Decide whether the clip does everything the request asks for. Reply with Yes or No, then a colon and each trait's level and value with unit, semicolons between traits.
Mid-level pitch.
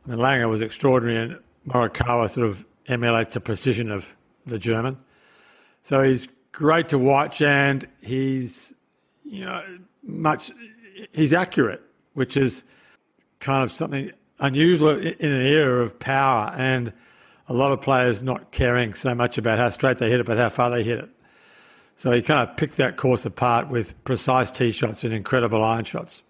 No: low, 130 Hz